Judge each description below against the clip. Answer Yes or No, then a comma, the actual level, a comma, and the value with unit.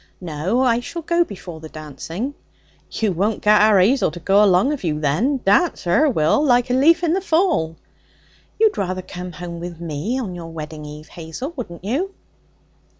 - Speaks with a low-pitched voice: No, high, 195 Hz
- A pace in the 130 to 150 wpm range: No, average, 185 wpm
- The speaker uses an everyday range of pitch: No, wide, 8.1 semitones